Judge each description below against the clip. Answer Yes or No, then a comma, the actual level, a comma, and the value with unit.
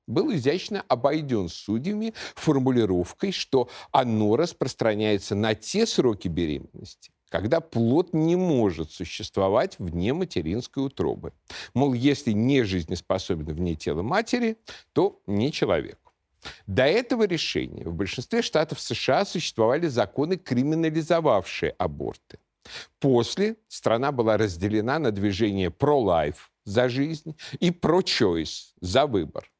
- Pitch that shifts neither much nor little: No, wide, 8.1 semitones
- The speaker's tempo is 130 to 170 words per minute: No, slow, 110 wpm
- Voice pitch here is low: Yes, low, 130 Hz